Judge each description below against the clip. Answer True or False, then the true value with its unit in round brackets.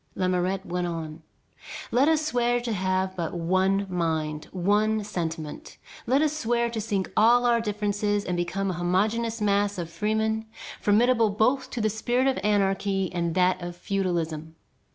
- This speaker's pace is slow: False (155 wpm)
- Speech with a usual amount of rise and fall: True (3.9 semitones)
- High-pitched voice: True (200 Hz)